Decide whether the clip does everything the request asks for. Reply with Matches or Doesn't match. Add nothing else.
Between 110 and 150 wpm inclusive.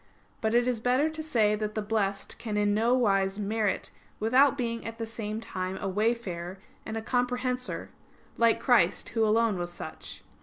Doesn't match